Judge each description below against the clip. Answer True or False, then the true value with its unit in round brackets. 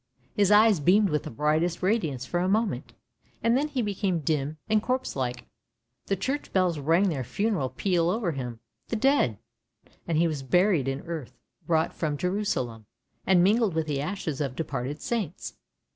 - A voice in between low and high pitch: True (170 Hz)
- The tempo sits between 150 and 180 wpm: True (175 wpm)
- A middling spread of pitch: False (6.1 semitones)